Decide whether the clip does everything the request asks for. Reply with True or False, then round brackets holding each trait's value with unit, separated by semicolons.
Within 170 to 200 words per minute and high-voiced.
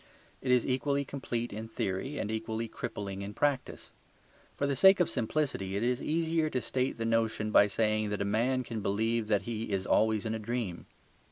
False (195 wpm; 115 Hz)